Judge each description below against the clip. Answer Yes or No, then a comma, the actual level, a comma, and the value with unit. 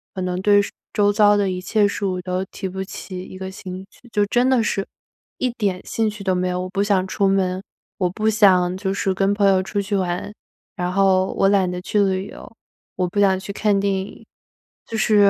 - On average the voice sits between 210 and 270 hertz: No, high, 195 Hz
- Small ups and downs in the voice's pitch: Yes, narrow, 1.7 semitones